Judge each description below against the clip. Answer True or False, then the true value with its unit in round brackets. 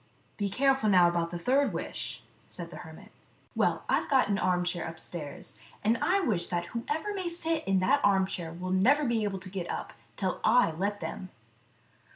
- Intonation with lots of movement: True (6.3 semitones)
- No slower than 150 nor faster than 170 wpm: False (195 wpm)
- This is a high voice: True (195 Hz)